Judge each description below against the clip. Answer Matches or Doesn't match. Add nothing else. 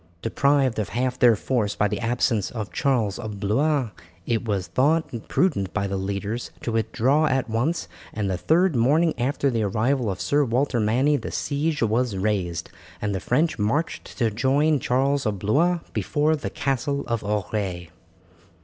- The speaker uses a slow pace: Doesn't match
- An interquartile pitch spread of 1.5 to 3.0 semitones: Doesn't match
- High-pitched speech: Doesn't match